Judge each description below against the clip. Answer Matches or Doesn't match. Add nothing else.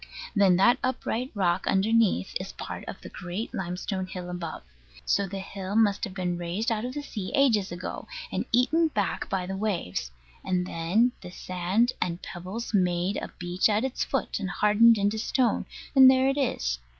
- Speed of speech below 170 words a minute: Doesn't match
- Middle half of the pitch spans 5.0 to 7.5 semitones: Doesn't match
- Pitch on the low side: Doesn't match